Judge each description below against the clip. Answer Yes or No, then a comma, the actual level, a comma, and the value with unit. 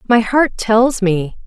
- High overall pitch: Yes, high, 220 Hz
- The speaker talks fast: No, average, 165 wpm